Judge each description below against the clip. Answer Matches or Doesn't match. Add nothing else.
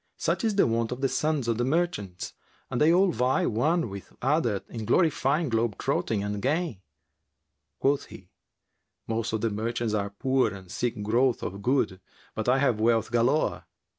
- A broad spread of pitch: Doesn't match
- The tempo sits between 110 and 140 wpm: Doesn't match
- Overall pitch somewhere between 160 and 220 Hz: Doesn't match